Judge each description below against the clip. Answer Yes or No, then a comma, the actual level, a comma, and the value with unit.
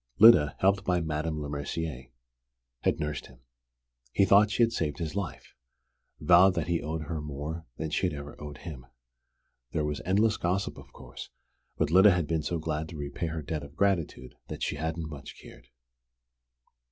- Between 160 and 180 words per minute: Yes, average, 175 wpm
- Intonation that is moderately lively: Yes, average, 3.4 semitones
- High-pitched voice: No, very low, 80 Hz